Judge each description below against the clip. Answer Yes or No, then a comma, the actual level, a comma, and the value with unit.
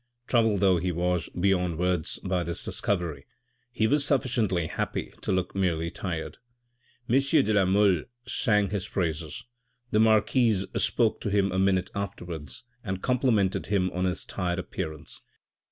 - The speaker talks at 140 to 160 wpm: Yes, average, 150 wpm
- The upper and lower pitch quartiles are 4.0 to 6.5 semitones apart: No, average, 3.0 semitones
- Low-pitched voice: Yes, very low, 95 Hz